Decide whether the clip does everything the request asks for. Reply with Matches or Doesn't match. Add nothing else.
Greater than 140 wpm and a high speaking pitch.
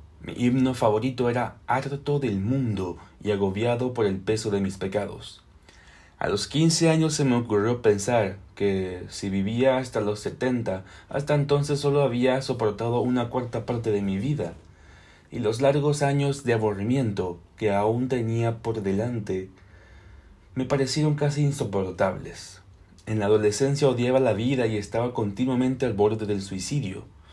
Doesn't match